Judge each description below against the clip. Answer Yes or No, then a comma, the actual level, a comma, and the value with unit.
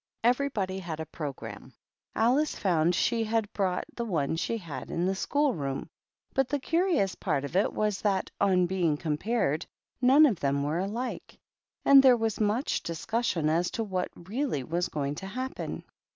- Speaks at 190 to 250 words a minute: No, average, 175 wpm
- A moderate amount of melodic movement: No, wide, 6.6 semitones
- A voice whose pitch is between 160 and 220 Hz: Yes, high, 190 Hz